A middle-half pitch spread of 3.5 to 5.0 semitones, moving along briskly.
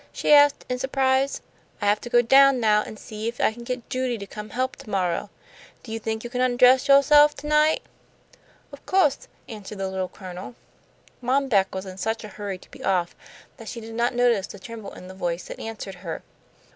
Yes: average, 4.5 semitones; fast, 215 wpm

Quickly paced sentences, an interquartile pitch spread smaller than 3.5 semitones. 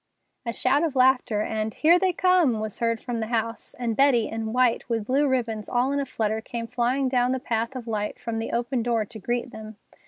Yes: fast, 225 wpm; average, 2.7 semitones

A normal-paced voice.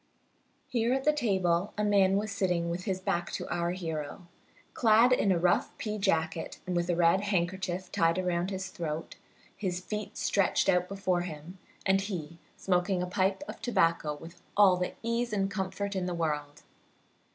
Yes: average, 175 wpm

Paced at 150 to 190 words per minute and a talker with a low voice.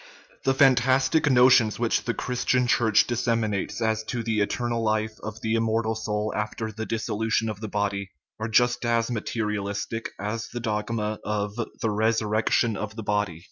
Yes: average, 165 wpm; low, 110 Hz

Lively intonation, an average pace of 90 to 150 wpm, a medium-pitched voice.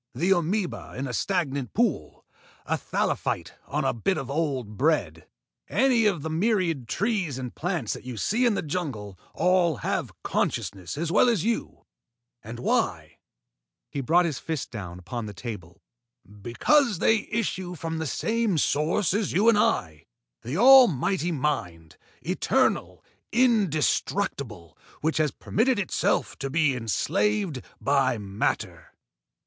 Yes: wide, 8.3 semitones; average, 145 wpm; medium, 160 Hz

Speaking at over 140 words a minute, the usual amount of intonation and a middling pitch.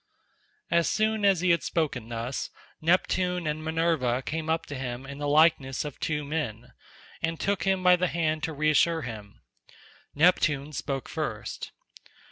Yes: average, 155 wpm; average, 3.9 semitones; medium, 155 Hz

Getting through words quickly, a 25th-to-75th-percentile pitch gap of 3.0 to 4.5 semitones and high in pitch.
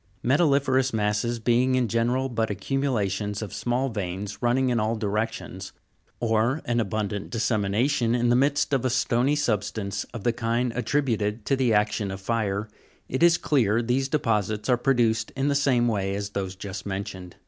No: fast, 215 wpm; average, 3.7 semitones; low, 115 Hz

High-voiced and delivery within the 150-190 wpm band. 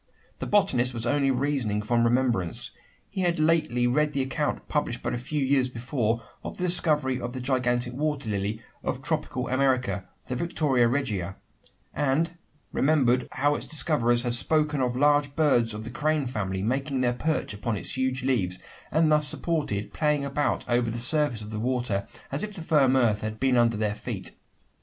No: low, 130 Hz; average, 180 wpm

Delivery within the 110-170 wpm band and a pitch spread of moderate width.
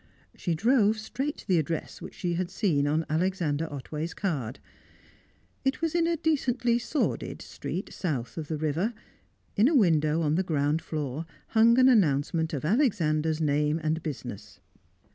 No: average, 160 wpm; wide, 6.6 semitones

